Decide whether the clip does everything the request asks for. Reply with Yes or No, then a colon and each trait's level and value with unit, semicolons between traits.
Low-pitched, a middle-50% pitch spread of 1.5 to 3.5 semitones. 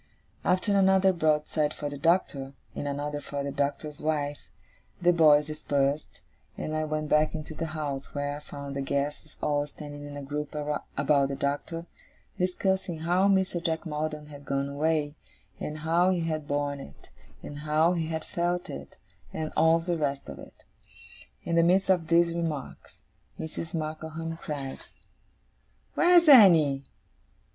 No: medium, 155 Hz; narrow, 2.6 semitones